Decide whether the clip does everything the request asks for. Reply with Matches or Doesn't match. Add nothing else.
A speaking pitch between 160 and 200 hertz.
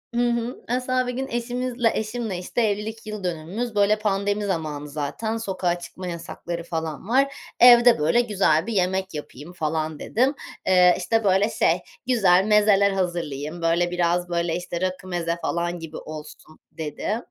Matches